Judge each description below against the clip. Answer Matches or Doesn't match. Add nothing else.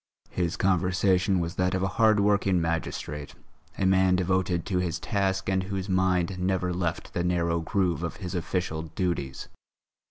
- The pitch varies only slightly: Matches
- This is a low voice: Matches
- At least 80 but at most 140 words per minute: Doesn't match